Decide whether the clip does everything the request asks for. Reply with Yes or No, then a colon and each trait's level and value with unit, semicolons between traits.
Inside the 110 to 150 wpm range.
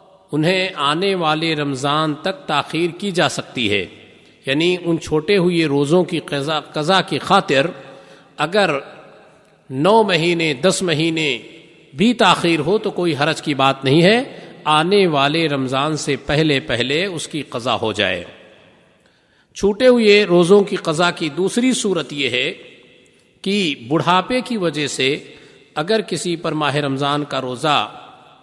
Yes: average, 140 wpm